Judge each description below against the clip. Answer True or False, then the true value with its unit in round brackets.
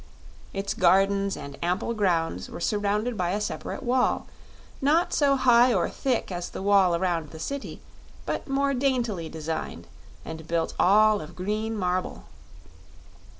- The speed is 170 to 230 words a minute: False (145 wpm)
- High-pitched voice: True (200 Hz)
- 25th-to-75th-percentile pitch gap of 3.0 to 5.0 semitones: False (5.5 semitones)